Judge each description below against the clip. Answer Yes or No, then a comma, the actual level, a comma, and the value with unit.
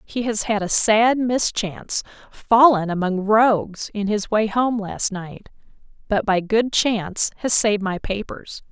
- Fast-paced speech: No, average, 160 wpm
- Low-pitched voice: No, high, 210 Hz